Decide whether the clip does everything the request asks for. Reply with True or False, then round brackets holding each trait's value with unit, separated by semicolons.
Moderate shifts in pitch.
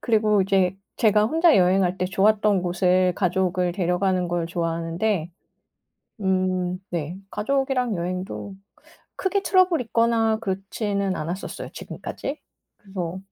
True (3.1 semitones)